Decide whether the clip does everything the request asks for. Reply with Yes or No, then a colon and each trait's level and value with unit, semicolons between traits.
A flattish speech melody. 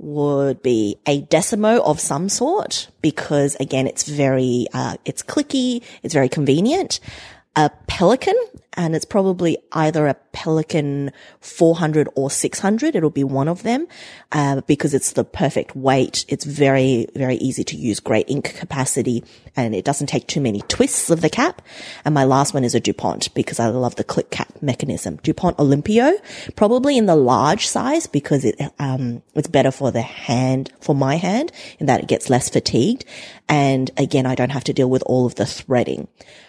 No: average, 4.2 semitones